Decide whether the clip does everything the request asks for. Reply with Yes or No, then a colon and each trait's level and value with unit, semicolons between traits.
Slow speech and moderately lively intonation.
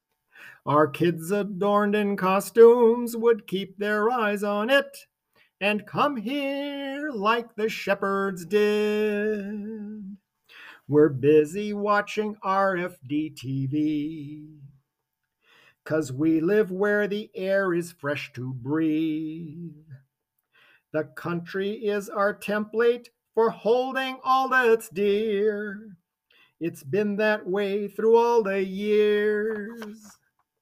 Yes: slow, 100 wpm; average, 4.9 semitones